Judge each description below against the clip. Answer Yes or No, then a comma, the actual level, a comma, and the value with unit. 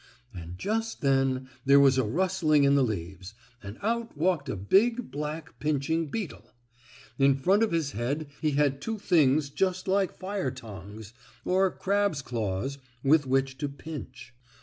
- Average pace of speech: Yes, average, 160 wpm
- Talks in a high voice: No, medium, 140 Hz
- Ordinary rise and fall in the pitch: No, wide, 6.2 semitones